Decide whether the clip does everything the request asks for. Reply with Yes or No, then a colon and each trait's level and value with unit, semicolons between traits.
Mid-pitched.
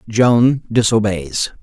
No: low, 110 Hz